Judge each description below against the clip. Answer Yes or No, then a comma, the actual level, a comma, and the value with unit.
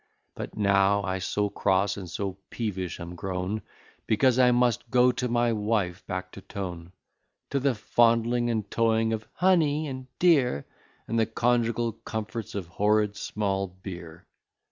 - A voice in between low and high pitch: No, low, 110 Hz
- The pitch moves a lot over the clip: No, average, 3.7 semitones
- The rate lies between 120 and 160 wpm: Yes, average, 150 wpm